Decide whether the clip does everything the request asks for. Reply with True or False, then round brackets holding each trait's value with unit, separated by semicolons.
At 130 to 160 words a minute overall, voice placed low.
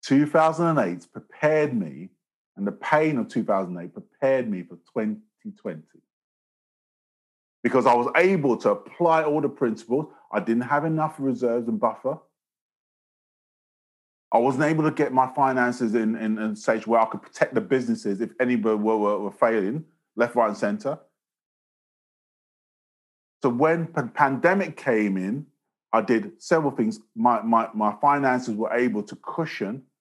True (150 wpm; 125 Hz)